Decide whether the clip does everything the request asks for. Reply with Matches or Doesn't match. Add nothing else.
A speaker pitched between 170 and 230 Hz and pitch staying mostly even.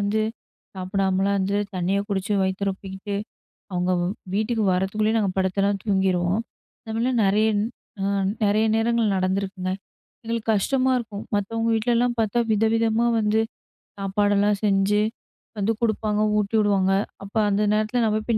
Matches